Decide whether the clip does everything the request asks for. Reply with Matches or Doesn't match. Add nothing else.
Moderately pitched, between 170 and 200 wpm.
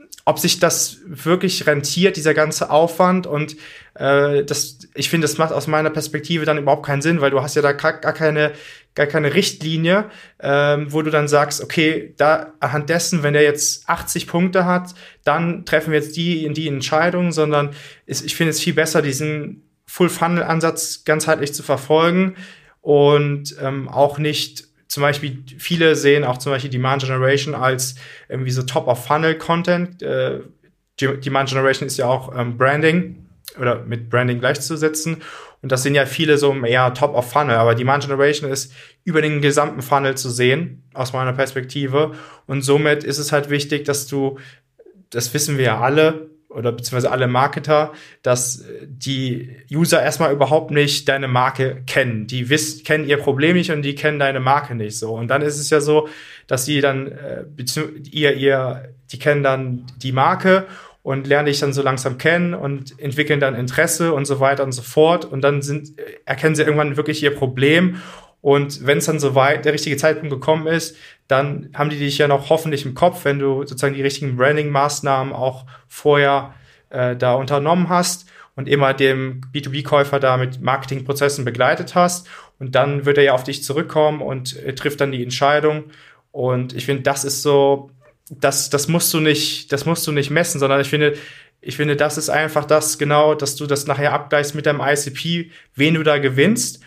Matches